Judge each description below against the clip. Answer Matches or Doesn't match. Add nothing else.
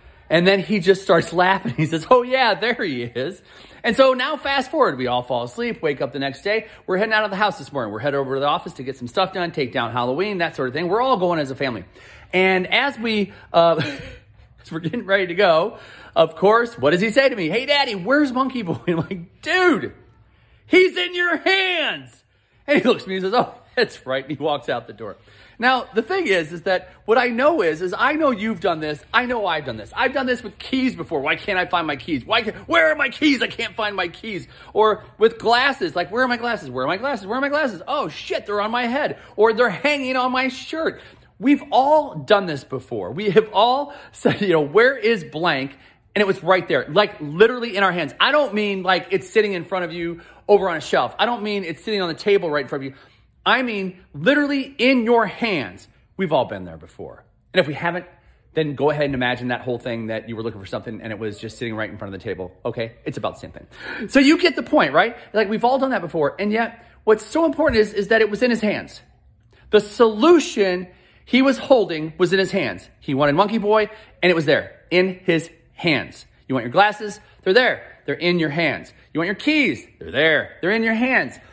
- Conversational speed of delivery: Doesn't match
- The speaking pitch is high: Matches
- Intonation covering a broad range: Matches